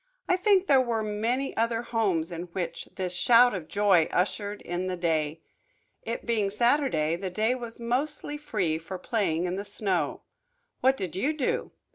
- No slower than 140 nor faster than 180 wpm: Yes, average, 170 wpm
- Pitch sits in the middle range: No, high, 210 Hz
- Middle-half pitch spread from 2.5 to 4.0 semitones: No, average, 5.3 semitones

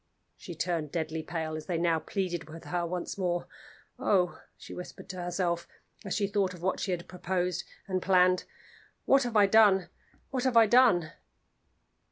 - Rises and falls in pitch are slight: Yes, narrow, 2.3 semitones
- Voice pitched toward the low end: No, medium, 180 Hz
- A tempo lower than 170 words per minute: No, average, 175 wpm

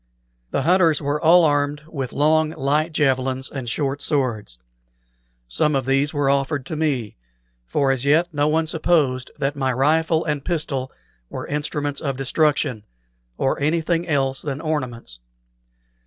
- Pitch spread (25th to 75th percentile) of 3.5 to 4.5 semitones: No, average, 2.7 semitones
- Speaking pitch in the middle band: Yes, medium, 145 Hz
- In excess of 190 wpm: No, average, 145 wpm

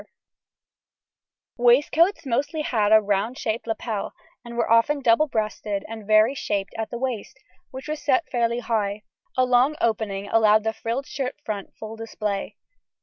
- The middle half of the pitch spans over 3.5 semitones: No, average, 3.2 semitones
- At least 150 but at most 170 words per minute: Yes, average, 155 wpm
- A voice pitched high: Yes, high, 230 Hz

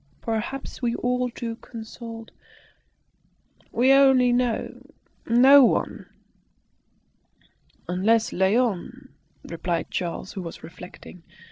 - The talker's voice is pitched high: Yes, high, 230 Hz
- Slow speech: Yes, slow, 95 wpm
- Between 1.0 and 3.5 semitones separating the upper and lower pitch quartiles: No, average, 4.7 semitones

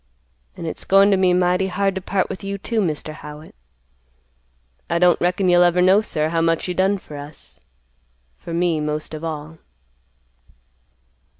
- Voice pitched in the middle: Yes, medium, 175 Hz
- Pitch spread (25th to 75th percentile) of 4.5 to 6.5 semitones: No, average, 3.3 semitones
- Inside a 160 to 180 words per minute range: Yes, average, 170 wpm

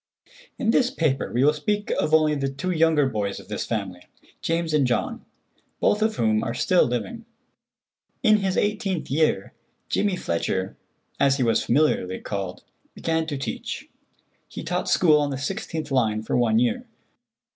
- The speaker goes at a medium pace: Yes, average, 165 wpm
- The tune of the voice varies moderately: No, wide, 7.2 semitones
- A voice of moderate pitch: Yes, medium, 150 Hz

